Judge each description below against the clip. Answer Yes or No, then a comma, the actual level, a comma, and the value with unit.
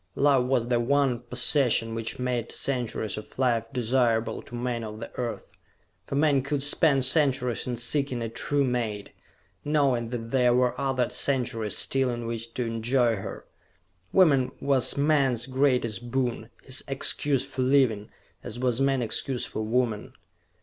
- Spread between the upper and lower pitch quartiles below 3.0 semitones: Yes, narrow, 2.6 semitones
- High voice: No, low, 125 Hz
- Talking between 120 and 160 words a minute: Yes, average, 155 wpm